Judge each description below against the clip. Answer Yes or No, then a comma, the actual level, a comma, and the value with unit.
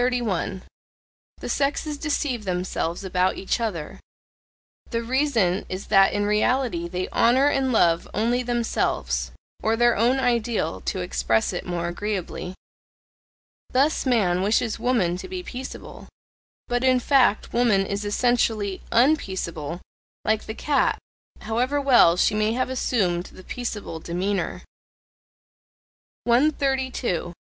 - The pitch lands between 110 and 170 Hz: No, high, 220 Hz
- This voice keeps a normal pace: No, slow, 120 wpm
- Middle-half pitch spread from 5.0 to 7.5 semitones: Yes, wide, 5.4 semitones